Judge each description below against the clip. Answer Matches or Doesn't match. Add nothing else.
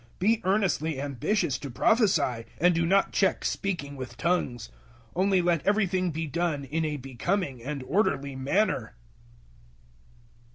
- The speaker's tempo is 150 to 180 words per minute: Doesn't match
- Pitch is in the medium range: Matches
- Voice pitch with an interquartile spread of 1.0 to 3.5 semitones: Doesn't match